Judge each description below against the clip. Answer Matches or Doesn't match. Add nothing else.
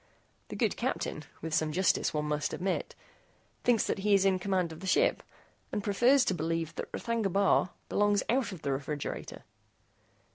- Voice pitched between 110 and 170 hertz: Doesn't match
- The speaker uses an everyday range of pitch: Matches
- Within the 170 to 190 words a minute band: Matches